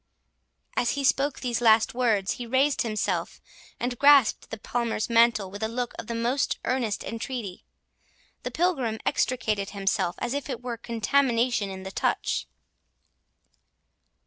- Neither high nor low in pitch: No, high, 235 Hz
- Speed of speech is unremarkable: Yes, average, 145 wpm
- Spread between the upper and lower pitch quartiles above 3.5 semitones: No, average, 2.8 semitones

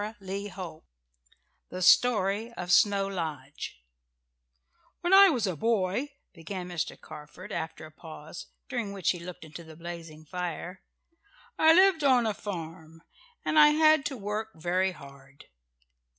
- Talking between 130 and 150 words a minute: Yes, average, 140 wpm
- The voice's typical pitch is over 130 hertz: Yes, medium, 185 Hz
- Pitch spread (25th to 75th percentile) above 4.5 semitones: Yes, average, 5.3 semitones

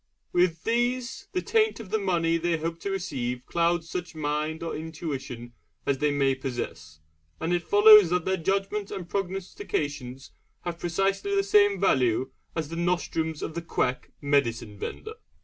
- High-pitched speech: No, medium, 170 Hz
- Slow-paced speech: No, average, 160 wpm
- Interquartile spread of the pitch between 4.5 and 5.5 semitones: Yes, average, 5.2 semitones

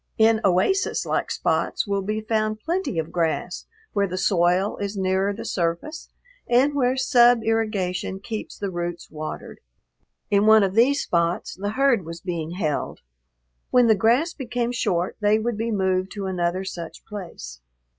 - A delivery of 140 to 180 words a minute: Yes, average, 160 wpm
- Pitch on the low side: No, high, 200 Hz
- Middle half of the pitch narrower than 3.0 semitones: No, average, 4.0 semitones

